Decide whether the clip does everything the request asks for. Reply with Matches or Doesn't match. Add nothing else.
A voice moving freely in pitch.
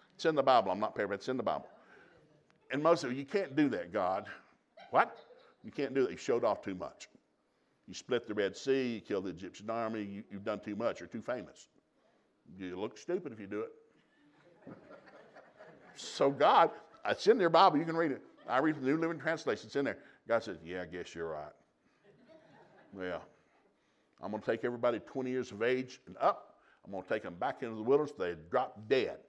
Matches